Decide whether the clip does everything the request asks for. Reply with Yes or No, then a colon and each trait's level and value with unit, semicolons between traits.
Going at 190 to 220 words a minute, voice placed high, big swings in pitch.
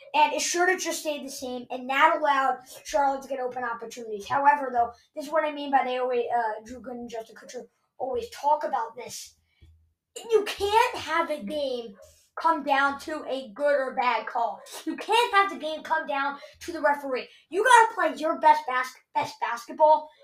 No: average, 200 wpm; very high, 285 Hz; average, 4.0 semitones